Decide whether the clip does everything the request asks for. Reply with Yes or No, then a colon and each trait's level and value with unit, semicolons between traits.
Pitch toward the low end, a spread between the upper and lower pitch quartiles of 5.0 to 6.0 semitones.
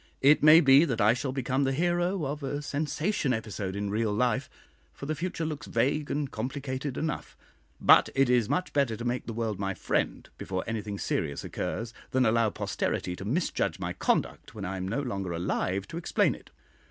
Yes: low, 125 Hz; average, 5.3 semitones